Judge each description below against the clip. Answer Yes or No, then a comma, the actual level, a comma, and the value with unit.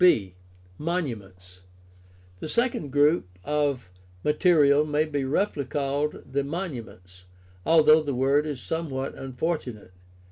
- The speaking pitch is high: No, medium, 140 Hz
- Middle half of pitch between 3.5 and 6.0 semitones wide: Yes, average, 5.1 semitones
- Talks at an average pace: No, slow, 120 wpm